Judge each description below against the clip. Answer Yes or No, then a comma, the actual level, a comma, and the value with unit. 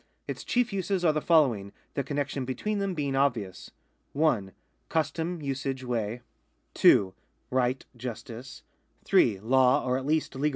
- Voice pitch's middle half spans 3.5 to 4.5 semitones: Yes, average, 4.2 semitones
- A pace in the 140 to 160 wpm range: Yes, average, 150 wpm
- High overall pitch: No, low, 135 Hz